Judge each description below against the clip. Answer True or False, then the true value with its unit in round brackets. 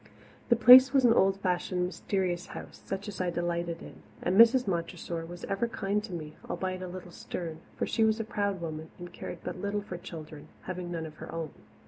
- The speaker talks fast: True (210 wpm)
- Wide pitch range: False (2.9 semitones)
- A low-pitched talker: False (180 Hz)